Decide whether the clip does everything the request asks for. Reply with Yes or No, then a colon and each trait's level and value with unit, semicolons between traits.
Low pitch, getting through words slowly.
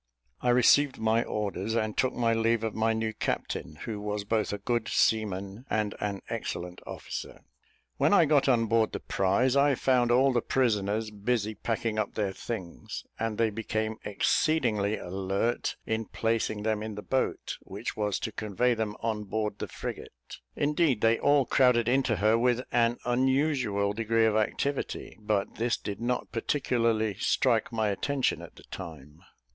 No: low, 110 Hz; average, 165 wpm